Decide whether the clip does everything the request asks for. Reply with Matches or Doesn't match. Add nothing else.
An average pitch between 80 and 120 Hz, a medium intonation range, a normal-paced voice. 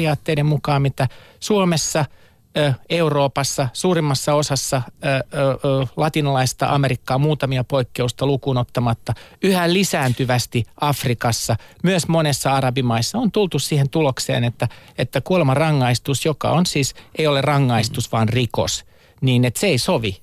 Doesn't match